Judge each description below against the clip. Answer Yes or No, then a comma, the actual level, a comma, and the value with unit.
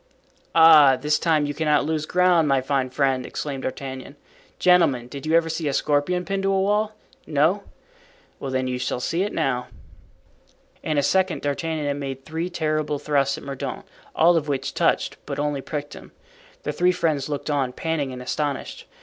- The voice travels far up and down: No, average, 3.1 semitones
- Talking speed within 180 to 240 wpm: Yes, average, 185 wpm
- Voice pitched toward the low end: No, medium, 150 Hz